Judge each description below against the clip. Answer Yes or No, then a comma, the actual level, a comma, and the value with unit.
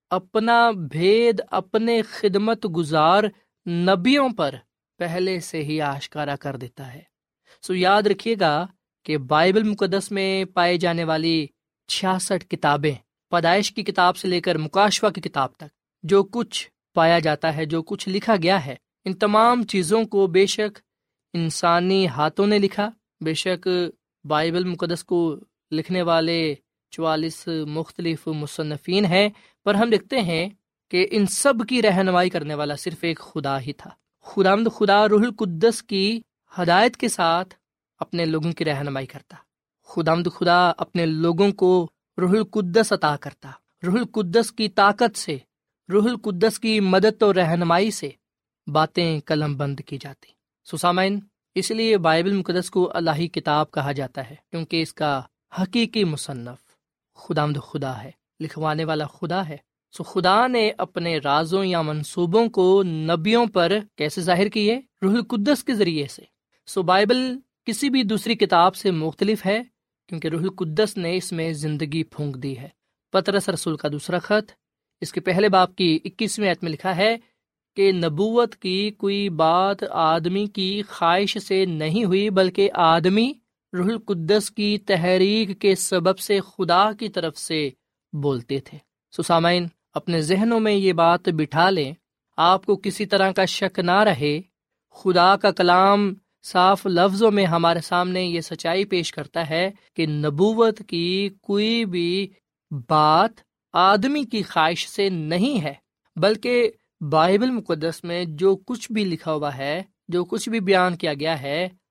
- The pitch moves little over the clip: No, average, 4.1 semitones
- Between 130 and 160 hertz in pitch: No, medium, 180 Hz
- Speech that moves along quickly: No, average, 150 wpm